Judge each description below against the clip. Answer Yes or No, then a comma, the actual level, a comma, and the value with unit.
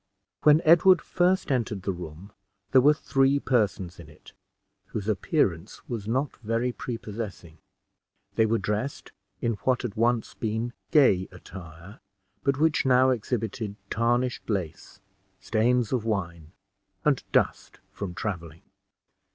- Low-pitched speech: Yes, low, 110 Hz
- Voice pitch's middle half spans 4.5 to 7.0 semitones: Yes, average, 4.9 semitones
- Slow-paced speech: Yes, slow, 125 wpm